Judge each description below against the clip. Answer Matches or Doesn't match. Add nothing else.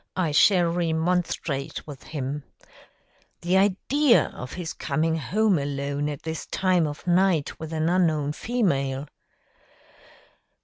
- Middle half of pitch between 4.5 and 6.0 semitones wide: Doesn't match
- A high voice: Doesn't match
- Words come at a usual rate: Doesn't match